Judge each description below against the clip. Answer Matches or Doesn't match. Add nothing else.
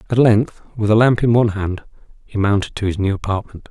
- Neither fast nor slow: Doesn't match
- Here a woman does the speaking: Doesn't match